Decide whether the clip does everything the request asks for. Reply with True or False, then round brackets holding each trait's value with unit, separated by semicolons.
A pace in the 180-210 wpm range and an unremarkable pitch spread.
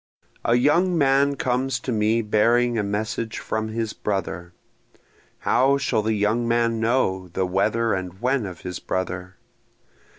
False (145 wpm; 3.5 semitones)